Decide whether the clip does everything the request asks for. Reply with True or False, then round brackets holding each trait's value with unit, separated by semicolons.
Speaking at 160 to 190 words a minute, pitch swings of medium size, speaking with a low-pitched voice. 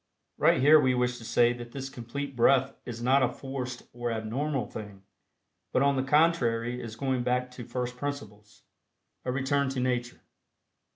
False (175 wpm; 2.3 semitones; 125 Hz)